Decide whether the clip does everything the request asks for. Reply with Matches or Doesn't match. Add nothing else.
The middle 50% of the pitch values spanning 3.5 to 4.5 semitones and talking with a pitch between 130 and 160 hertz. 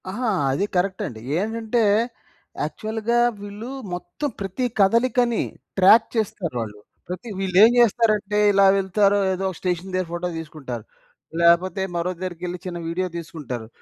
Doesn't match